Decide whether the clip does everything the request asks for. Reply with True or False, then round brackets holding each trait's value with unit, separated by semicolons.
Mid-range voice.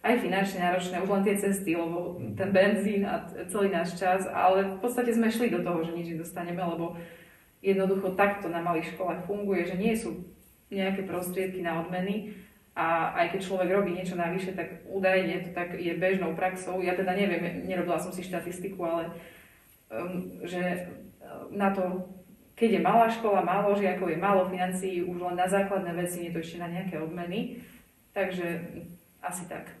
True (180 Hz)